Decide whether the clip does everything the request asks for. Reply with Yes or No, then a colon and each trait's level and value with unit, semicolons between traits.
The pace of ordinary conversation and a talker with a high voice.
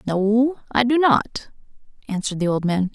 Yes: average, 165 wpm; high, 220 Hz